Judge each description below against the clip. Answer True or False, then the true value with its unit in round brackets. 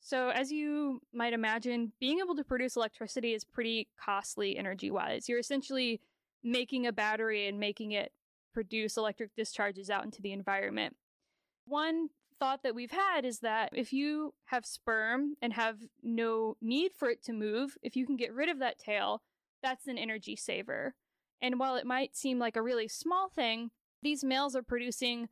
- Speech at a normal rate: True (180 wpm)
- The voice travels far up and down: False (3.4 semitones)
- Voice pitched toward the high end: True (245 Hz)